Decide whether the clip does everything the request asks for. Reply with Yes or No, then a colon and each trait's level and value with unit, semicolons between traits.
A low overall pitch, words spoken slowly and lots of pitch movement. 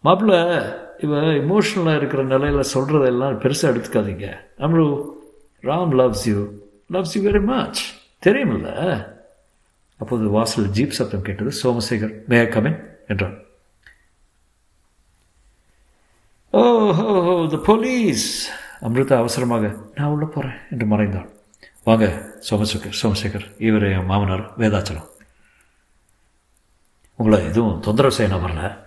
No: low, 115 Hz; average, 100 wpm; wide, 6.3 semitones